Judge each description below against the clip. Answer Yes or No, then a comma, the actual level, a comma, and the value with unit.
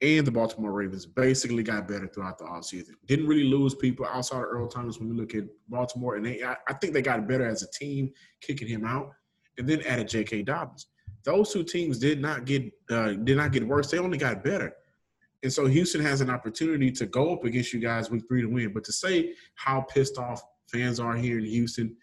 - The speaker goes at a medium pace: No, fast, 230 wpm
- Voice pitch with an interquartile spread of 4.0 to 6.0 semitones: No, average, 3.4 semitones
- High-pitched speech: No, low, 125 Hz